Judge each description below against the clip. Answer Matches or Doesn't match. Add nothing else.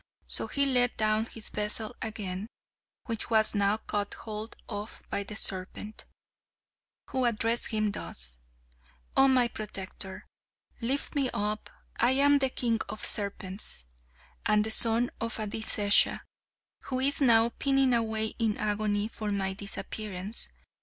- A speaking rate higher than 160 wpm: Doesn't match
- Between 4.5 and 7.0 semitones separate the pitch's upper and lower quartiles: Doesn't match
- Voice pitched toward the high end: Matches